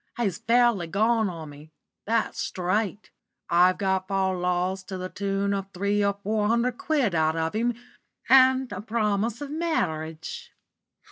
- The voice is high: Yes, high, 200 Hz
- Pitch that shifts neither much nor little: Yes, average, 4.1 semitones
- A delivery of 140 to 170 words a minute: Yes, average, 150 wpm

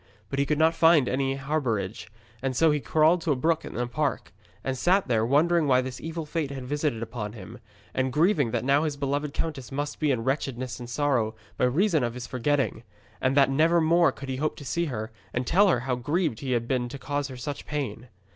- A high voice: No, medium, 140 Hz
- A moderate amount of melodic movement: Yes, average, 3.7 semitones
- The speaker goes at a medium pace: No, fast, 230 wpm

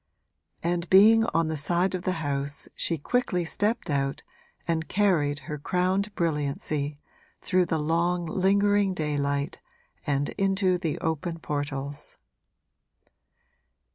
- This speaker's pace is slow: Yes, slow, 115 wpm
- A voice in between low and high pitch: Yes, medium, 165 Hz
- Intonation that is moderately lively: Yes, average, 4.3 semitones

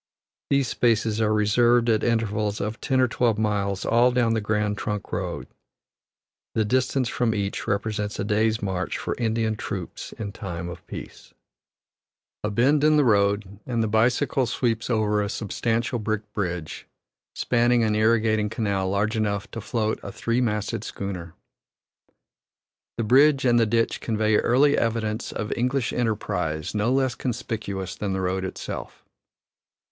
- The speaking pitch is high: No, low, 110 Hz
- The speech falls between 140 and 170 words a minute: Yes, average, 150 wpm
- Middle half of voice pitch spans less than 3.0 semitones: Yes, narrow, 2.5 semitones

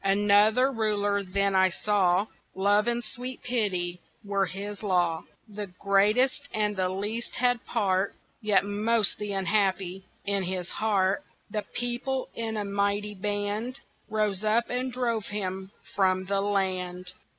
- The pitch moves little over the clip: Yes, narrow, 2.2 semitones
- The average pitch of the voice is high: Yes, high, 205 Hz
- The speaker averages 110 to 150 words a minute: Yes, average, 140 wpm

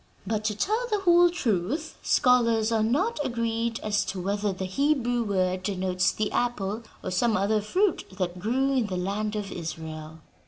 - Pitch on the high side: Yes, high, 215 Hz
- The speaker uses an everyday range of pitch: Yes, average, 4.8 semitones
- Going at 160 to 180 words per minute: Yes, average, 170 wpm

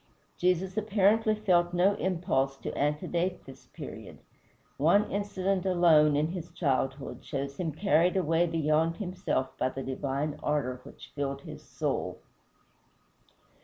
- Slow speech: Yes, slow, 130 wpm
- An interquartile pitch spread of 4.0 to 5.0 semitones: Yes, average, 4.5 semitones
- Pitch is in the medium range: Yes, medium, 165 Hz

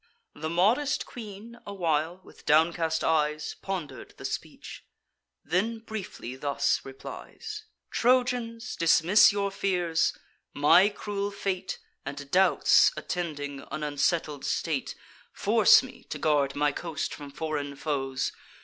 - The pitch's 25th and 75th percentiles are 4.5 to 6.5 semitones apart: Yes, average, 5.3 semitones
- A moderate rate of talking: No, slow, 120 wpm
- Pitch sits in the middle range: Yes, medium, 165 Hz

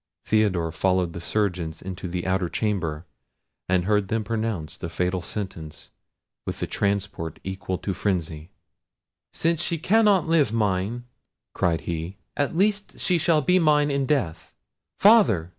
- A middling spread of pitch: No, wide, 8.4 semitones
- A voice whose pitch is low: Yes, low, 100 Hz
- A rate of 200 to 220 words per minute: No, average, 140 wpm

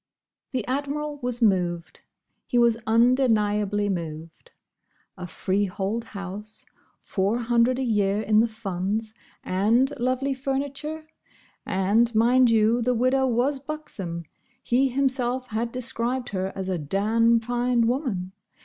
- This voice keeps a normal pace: No, slow, 120 wpm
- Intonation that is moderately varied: Yes, average, 4.0 semitones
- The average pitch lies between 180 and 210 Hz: No, high, 230 Hz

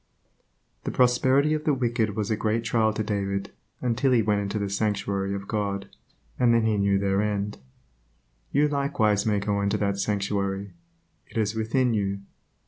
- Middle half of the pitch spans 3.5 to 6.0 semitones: No, average, 2.7 semitones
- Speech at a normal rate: Yes, average, 170 wpm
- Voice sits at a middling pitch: No, low, 105 Hz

